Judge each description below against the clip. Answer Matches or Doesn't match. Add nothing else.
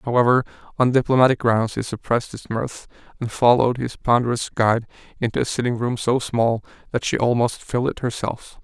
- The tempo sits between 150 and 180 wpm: Matches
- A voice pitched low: Matches